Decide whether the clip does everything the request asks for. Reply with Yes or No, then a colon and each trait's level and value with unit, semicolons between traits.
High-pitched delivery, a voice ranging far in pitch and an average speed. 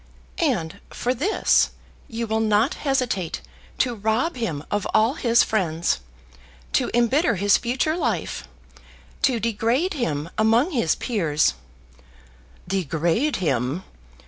No: high, 220 Hz; wide, 6.9 semitones; slow, 120 wpm